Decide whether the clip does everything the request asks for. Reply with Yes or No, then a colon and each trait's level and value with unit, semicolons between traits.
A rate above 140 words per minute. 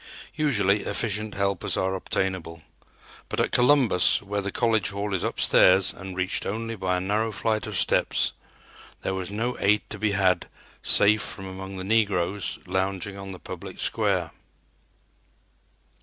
Yes: average, 150 wpm